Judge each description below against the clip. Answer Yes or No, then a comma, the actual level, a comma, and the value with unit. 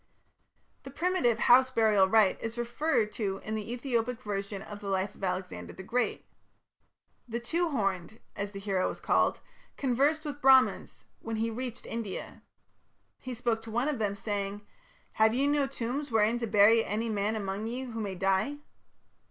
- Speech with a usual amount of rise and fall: Yes, average, 3.6 semitones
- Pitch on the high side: Yes, high, 225 Hz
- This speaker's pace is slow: No, average, 170 wpm